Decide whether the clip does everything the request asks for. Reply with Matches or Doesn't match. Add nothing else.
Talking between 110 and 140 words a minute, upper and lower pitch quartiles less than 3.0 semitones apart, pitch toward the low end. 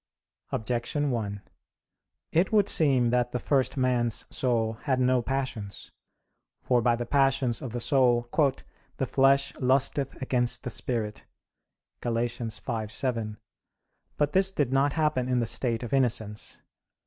Matches